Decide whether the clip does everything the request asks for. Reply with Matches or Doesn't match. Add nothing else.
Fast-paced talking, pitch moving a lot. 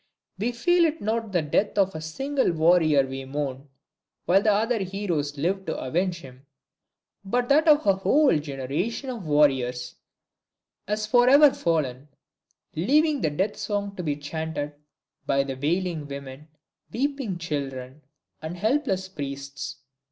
Doesn't match